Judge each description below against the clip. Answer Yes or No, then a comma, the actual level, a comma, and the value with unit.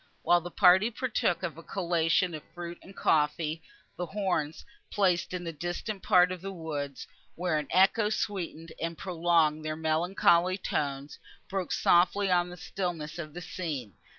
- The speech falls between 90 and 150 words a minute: No, average, 160 wpm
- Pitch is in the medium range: Yes, medium, 175 Hz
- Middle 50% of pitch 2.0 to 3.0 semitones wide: Yes, narrow, 2.5 semitones